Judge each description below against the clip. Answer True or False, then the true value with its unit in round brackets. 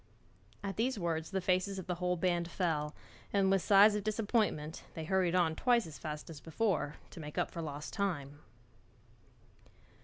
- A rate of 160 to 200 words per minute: True (175 wpm)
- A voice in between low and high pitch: True (180 Hz)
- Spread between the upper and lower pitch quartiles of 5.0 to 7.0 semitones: False (3.9 semitones)